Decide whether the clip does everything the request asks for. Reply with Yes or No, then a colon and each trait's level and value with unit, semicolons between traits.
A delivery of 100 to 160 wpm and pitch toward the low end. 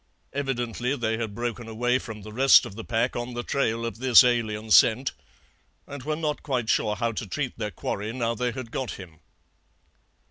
No: average, 190 wpm; low, 120 Hz